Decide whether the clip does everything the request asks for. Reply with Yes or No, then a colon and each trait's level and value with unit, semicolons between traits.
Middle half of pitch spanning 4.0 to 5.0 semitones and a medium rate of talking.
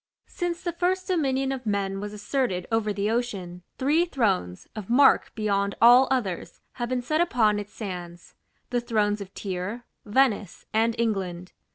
Yes: average, 4.7 semitones; average, 160 wpm